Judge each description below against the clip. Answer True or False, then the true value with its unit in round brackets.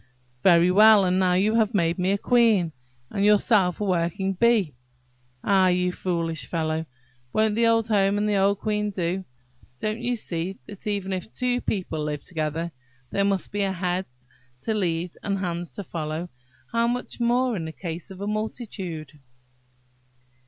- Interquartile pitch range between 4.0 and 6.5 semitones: False (3.6 semitones)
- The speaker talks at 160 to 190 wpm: True (170 wpm)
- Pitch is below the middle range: False (190 Hz)